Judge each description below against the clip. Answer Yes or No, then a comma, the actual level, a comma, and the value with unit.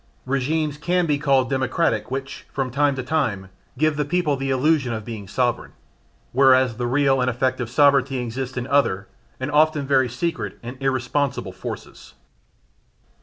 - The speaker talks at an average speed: Yes, average, 155 wpm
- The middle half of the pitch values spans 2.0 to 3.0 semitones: Yes, narrow, 2.6 semitones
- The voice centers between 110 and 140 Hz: Yes, low, 135 Hz